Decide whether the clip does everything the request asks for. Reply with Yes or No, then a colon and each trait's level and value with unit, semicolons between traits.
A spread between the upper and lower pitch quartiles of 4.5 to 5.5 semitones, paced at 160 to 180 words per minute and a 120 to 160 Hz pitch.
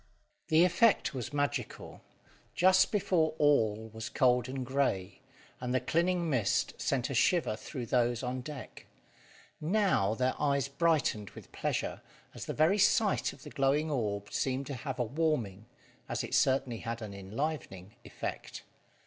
No: average, 5.1 semitones; average, 150 wpm; low, 135 Hz